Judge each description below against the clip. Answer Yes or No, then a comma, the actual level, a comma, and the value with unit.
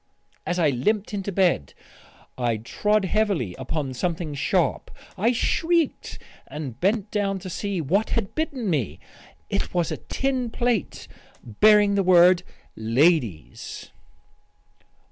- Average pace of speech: No, slow, 125 wpm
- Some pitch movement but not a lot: No, wide, 6.2 semitones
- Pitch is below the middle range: No, medium, 185 Hz